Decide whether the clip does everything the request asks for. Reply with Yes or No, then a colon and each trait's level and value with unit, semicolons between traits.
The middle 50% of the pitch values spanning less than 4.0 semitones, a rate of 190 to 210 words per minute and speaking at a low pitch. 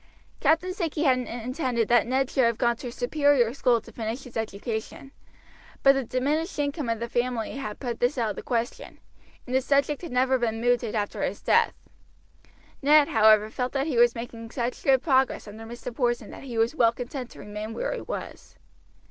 No: average, 2.9 semitones; average, 200 wpm; high, 245 Hz